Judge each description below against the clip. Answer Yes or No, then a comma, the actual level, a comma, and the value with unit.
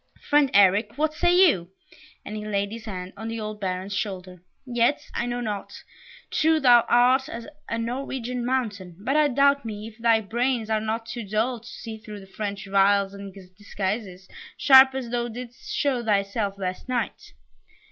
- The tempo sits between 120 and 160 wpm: No, average, 180 wpm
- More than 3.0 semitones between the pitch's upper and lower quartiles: Yes, average, 3.7 semitones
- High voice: Yes, high, 225 Hz